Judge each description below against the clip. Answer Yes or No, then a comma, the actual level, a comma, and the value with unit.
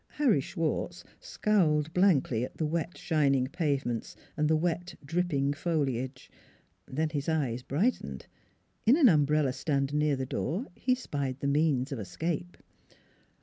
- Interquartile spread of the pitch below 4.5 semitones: Yes, average, 3.8 semitones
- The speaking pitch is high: No, medium, 150 Hz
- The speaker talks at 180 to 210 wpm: No, average, 140 wpm